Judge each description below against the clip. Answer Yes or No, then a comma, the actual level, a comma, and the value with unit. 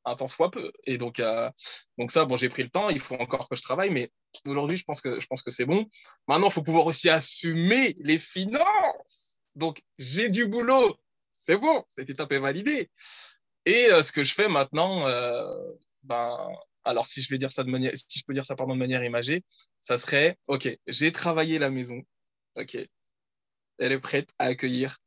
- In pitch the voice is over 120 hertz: Yes, medium, 140 Hz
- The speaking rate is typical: Yes, average, 205 wpm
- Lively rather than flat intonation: Yes, wide, 6.0 semitones